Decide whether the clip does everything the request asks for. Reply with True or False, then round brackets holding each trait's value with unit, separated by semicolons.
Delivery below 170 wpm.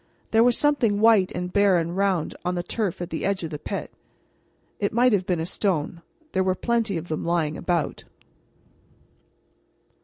False (180 wpm)